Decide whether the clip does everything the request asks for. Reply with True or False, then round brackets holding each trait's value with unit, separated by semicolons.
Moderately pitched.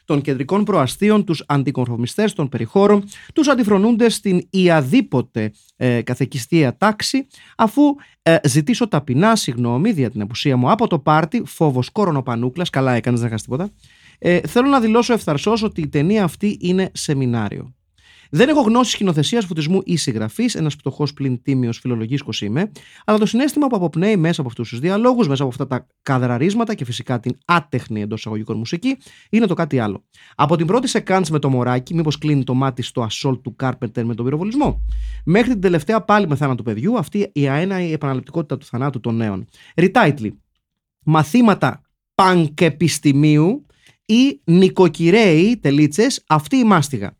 True (155 Hz)